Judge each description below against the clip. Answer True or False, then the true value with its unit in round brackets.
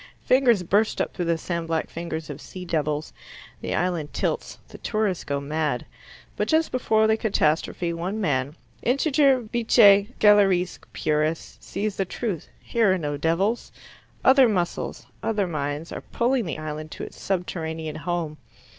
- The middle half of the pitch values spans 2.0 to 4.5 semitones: False (5.6 semitones)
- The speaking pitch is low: False (180 Hz)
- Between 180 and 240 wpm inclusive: False (155 wpm)